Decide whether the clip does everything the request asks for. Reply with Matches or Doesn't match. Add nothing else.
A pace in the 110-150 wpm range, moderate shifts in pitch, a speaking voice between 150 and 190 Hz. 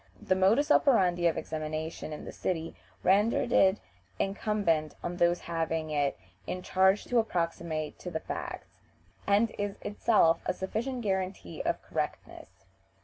Matches